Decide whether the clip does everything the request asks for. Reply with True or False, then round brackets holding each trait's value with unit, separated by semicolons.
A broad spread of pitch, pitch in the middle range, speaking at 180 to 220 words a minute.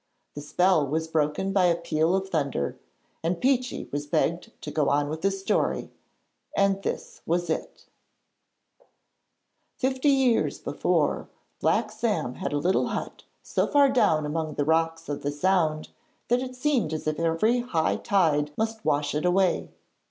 False (5.7 semitones; 170 Hz; 160 wpm)